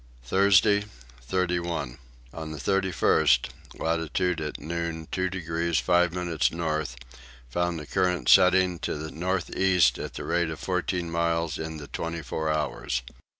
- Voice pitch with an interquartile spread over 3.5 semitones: No, narrow, 2.5 semitones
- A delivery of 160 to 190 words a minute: No, average, 145 wpm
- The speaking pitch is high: No, very low, 85 Hz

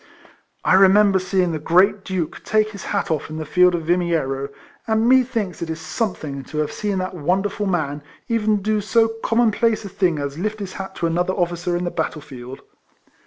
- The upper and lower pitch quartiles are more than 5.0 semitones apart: No, average, 4.4 semitones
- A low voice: No, medium, 185 Hz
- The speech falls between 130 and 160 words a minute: No, fast, 205 wpm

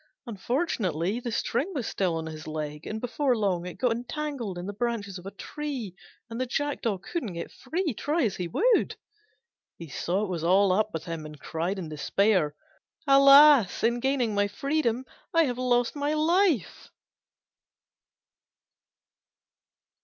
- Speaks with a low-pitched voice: No, high, 225 Hz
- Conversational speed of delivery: Yes, average, 155 wpm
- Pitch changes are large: Yes, wide, 7.3 semitones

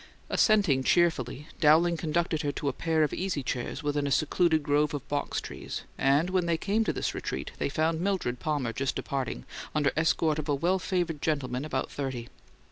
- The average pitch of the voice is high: No, medium, 150 Hz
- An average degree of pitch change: Yes, average, 3.4 semitones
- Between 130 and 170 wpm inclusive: No, average, 190 wpm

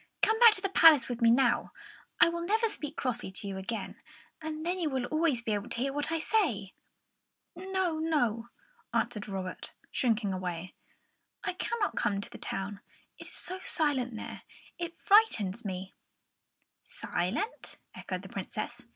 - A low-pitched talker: No, very high, 260 Hz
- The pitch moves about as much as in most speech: No, wide, 8.3 semitones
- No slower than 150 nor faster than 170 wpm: Yes, average, 165 wpm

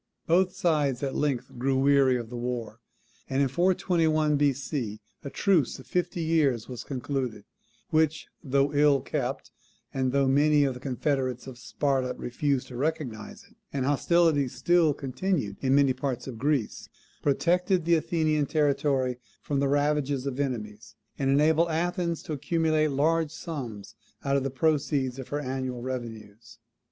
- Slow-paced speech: No, average, 155 wpm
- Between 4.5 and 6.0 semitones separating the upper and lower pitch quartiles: No, average, 3.3 semitones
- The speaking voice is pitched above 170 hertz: No, medium, 140 Hz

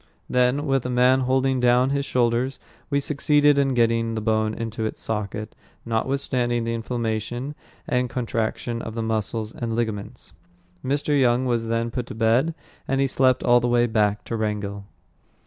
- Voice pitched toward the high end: No, low, 120 Hz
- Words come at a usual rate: Yes, average, 165 wpm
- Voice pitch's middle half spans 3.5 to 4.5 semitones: No, narrow, 2.6 semitones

